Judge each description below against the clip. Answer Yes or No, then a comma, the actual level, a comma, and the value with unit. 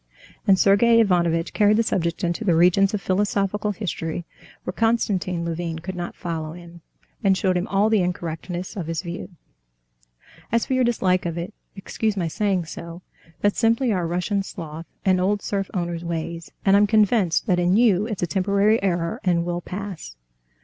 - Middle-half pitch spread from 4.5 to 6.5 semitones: No, average, 3.2 semitones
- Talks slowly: No, average, 175 wpm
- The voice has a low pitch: No, medium, 185 Hz